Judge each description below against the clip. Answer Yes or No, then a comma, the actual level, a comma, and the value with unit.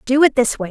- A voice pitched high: Yes, very high, 255 Hz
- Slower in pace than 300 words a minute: No, fast, 340 wpm